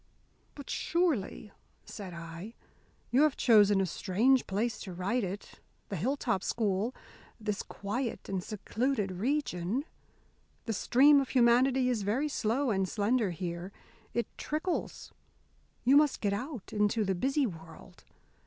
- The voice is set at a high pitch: Yes, high, 220 Hz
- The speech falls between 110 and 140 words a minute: Yes, slow, 135 wpm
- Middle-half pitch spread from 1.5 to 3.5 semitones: No, average, 5.3 semitones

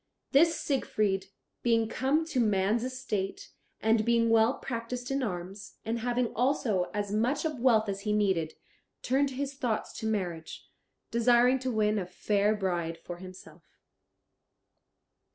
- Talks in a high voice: Yes, high, 225 Hz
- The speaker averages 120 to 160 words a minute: Yes, average, 140 wpm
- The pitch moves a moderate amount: Yes, average, 4.1 semitones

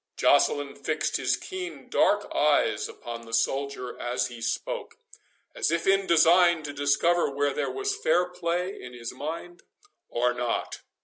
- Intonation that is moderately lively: No, wide, 6.1 semitones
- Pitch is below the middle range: No, medium, 155 Hz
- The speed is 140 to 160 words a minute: Yes, average, 150 wpm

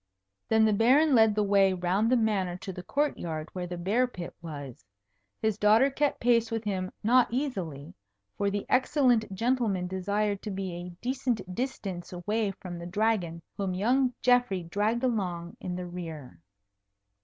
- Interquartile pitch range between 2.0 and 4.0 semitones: No, average, 4.7 semitones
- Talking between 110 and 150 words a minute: No, average, 165 wpm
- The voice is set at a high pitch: Yes, high, 200 Hz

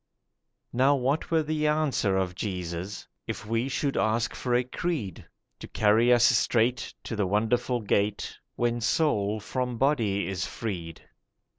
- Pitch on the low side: Yes, low, 115 Hz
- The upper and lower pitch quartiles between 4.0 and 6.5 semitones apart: Yes, average, 4.3 semitones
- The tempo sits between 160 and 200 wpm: No, average, 145 wpm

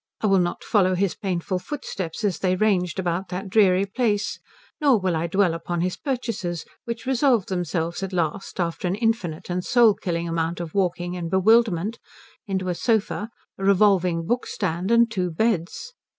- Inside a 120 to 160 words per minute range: No, average, 170 wpm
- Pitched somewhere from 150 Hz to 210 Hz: Yes, medium, 185 Hz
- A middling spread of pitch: Yes, average, 3.5 semitones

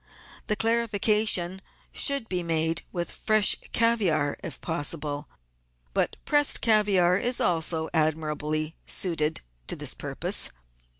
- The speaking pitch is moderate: Yes, medium, 175 Hz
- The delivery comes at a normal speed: No, slow, 115 wpm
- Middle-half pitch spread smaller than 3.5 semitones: No, wide, 5.4 semitones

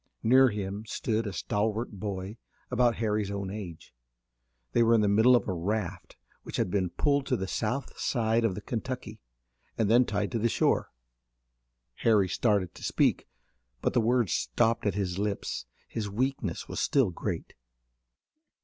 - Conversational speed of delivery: Yes, average, 165 wpm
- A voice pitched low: Yes, low, 105 Hz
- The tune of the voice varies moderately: Yes, average, 3.0 semitones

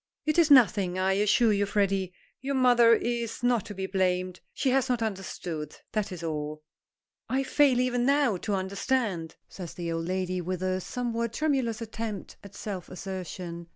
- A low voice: No, high, 200 Hz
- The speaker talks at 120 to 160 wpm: No, average, 170 wpm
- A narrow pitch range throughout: No, average, 4.8 semitones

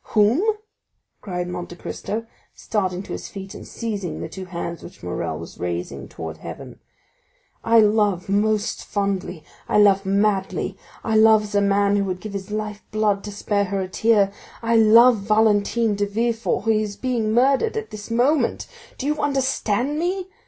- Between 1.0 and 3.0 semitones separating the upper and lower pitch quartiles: Yes, average, 2.7 semitones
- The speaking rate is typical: Yes, average, 160 wpm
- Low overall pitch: No, high, 205 Hz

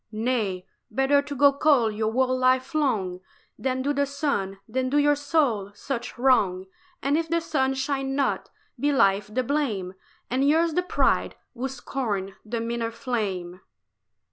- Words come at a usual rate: Yes, average, 160 wpm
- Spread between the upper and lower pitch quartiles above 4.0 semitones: Yes, average, 4.6 semitones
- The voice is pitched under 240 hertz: No, very high, 255 Hz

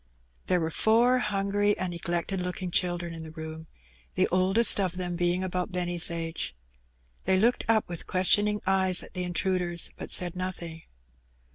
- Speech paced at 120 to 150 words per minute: No, average, 160 wpm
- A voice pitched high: No, medium, 180 Hz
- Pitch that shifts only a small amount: Yes, narrow, 1.9 semitones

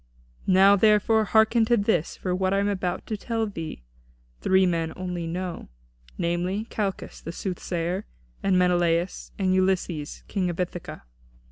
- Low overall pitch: No, medium, 185 Hz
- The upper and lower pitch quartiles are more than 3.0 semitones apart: No, narrow, 2.5 semitones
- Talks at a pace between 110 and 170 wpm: Yes, average, 145 wpm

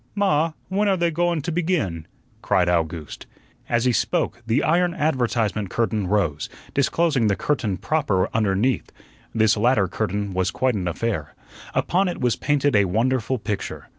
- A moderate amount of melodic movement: No, wide, 7.5 semitones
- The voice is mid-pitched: No, low, 115 Hz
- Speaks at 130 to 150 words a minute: No, average, 160 wpm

